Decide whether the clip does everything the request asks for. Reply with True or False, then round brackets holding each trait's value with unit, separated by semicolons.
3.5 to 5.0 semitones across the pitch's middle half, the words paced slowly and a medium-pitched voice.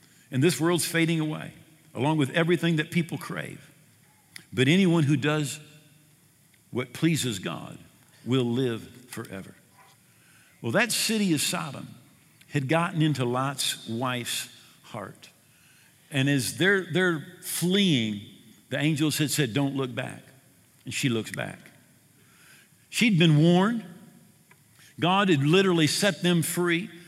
True (4.2 semitones; 125 wpm; 155 Hz)